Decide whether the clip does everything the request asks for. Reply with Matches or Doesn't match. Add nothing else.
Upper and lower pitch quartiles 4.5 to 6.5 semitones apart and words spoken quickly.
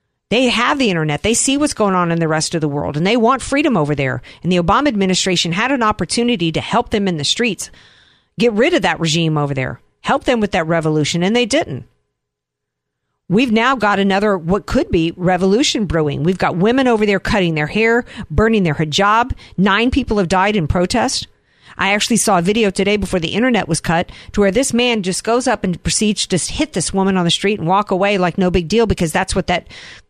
Matches